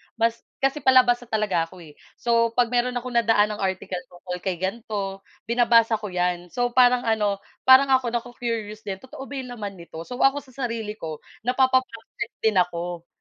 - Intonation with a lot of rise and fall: No, average, 4.2 semitones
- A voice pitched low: No, high, 230 Hz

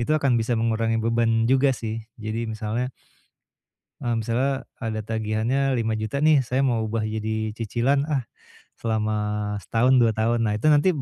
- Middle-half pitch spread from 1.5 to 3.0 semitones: Yes, narrow, 2.6 semitones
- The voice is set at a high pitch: No, low, 115 Hz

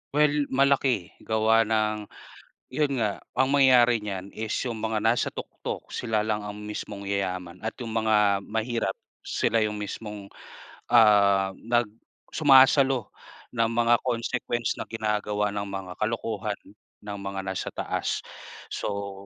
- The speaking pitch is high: No, low, 110 Hz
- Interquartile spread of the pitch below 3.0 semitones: Yes, narrow, 2.6 semitones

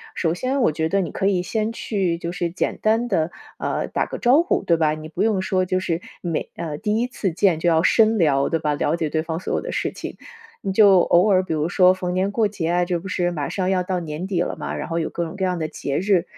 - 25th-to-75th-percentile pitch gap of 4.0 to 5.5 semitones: No, average, 3.1 semitones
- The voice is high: No, medium, 180 Hz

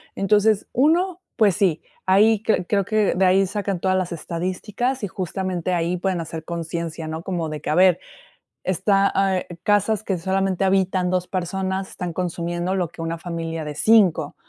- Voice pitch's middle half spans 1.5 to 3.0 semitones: Yes, narrow, 2.6 semitones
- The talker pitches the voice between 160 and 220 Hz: Yes, medium, 185 Hz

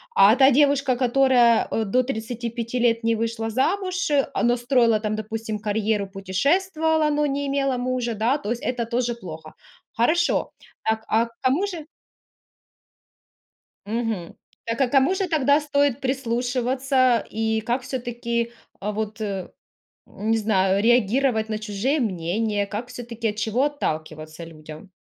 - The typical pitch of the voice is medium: No, high, 235 Hz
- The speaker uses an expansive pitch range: No, average, 3.6 semitones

